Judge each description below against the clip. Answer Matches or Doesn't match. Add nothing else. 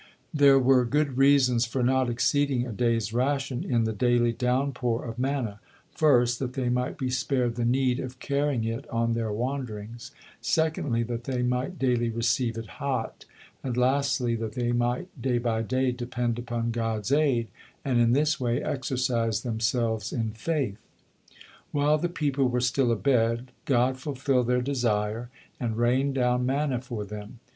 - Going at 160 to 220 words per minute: Matches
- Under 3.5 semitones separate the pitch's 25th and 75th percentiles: Matches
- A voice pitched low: Matches